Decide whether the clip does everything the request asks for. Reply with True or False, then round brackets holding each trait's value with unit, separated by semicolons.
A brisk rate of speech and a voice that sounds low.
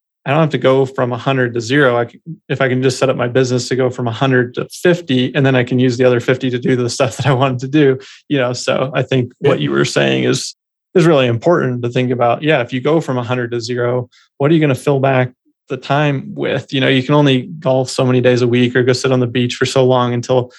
True (285 wpm; 130 Hz)